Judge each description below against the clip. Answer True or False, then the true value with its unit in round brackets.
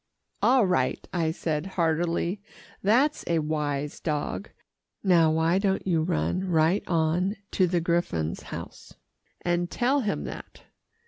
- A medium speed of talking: False (130 wpm)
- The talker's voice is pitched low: False (170 Hz)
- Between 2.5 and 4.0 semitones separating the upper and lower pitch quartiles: True (3.2 semitones)